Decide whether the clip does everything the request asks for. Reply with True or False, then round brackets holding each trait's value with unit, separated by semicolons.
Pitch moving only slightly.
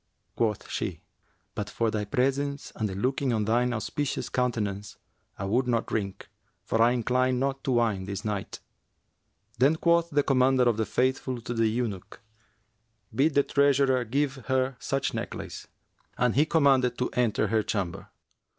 False (3.6 semitones)